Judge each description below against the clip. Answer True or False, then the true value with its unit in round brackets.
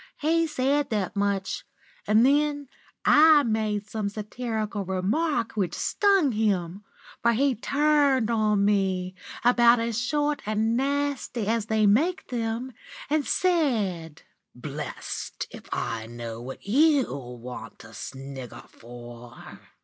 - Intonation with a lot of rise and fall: True (6.4 semitones)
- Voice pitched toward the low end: False (220 Hz)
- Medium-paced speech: False (120 wpm)